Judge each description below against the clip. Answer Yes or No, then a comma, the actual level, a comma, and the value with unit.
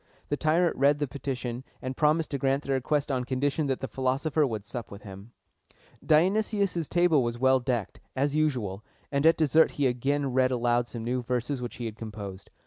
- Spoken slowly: No, average, 195 wpm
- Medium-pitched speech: No, low, 130 Hz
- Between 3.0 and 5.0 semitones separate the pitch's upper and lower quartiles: Yes, average, 3.5 semitones